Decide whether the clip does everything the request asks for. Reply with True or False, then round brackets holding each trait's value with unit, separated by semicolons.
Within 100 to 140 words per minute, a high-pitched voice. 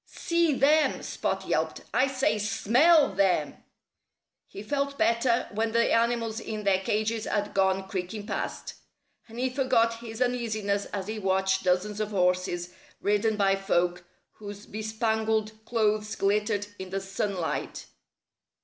True (135 wpm; 215 Hz)